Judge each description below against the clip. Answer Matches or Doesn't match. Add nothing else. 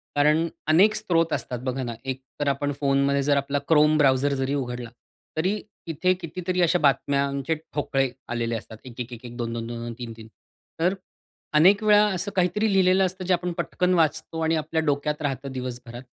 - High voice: Doesn't match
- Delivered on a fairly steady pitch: Doesn't match